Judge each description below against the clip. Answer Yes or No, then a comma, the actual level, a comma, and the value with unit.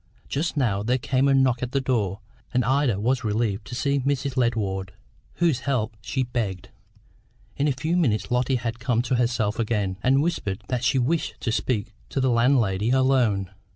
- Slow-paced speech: No, average, 185 wpm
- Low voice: Yes, low, 125 Hz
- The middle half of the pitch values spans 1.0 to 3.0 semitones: No, average, 3.5 semitones